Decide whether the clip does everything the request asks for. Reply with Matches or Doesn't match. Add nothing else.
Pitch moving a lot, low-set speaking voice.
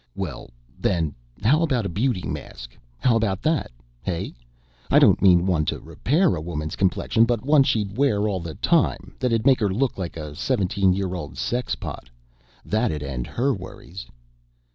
Matches